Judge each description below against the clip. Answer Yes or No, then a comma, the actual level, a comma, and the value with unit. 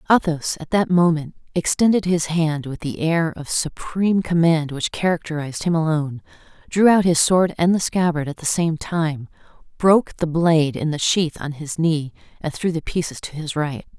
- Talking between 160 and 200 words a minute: Yes, average, 190 wpm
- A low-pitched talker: No, medium, 160 Hz